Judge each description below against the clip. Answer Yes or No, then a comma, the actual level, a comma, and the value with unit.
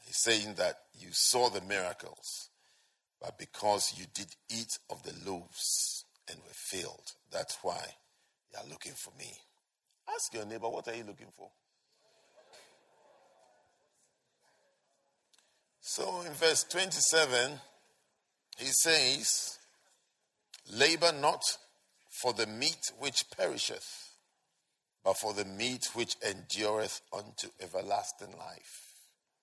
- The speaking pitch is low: Yes, low, 115 Hz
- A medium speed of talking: No, slow, 110 wpm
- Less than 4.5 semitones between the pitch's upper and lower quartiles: No, average, 5.2 semitones